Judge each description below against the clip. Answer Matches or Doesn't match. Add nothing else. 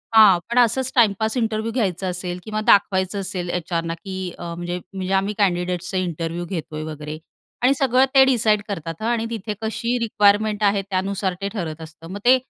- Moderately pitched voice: Doesn't match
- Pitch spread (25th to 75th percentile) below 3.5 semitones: Doesn't match